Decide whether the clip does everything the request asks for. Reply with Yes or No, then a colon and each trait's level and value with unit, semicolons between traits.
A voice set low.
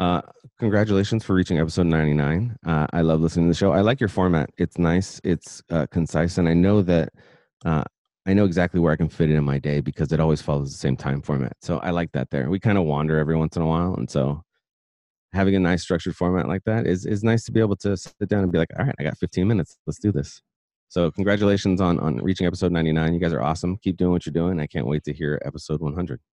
Yes: very low, 85 Hz